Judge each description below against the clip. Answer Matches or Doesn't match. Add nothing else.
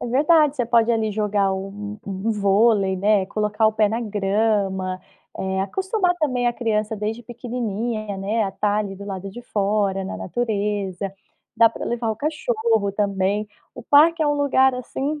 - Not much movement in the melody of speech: Doesn't match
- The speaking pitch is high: Matches